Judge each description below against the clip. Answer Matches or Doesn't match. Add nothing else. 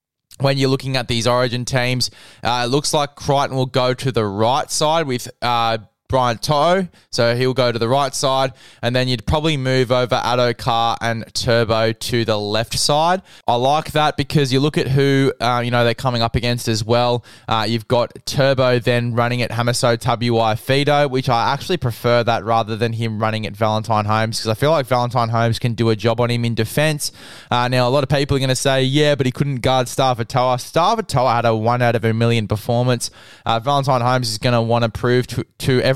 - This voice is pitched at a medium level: Doesn't match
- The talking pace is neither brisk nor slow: Doesn't match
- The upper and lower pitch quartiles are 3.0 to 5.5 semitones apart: Doesn't match